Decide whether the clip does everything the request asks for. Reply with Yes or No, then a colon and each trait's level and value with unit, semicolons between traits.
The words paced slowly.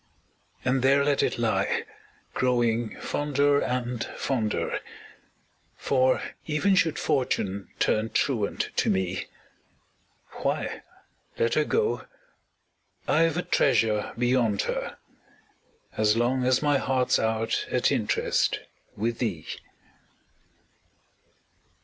Yes: slow, 100 wpm